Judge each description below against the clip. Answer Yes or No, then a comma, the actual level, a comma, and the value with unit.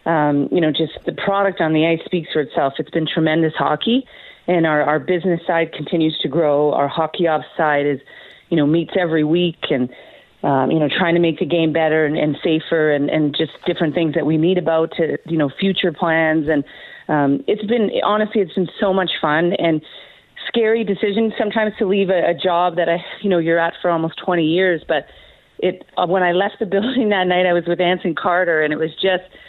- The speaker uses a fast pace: Yes, fast, 220 wpm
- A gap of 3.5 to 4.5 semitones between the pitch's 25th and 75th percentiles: No, average, 2.8 semitones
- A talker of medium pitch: Yes, medium, 170 Hz